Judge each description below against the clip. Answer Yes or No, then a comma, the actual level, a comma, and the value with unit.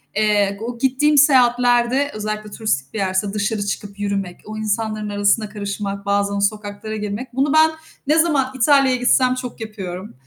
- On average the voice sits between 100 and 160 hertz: No, high, 215 Hz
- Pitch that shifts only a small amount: No, average, 3.8 semitones